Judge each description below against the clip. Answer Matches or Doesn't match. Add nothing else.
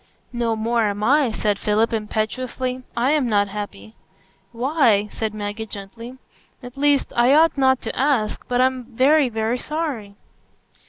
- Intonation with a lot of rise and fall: Doesn't match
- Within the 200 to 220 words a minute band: Doesn't match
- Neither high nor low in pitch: Doesn't match